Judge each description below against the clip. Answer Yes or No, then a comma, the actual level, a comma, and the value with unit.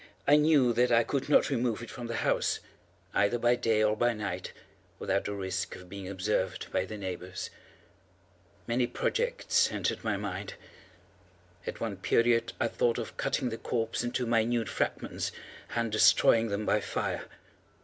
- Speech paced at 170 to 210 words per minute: No, average, 160 wpm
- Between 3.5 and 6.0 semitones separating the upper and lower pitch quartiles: No, average, 3.1 semitones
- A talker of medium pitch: No, low, 115 Hz